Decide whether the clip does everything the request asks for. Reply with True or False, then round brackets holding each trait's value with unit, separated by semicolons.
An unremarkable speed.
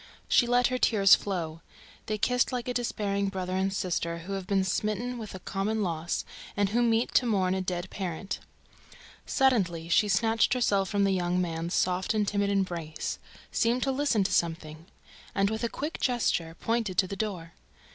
True (185 wpm)